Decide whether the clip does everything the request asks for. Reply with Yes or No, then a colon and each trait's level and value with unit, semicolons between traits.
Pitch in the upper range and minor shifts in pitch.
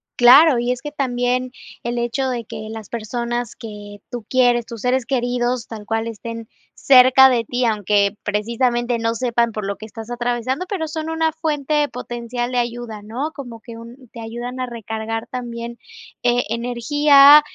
Yes: high, 240 Hz; narrow, 1.9 semitones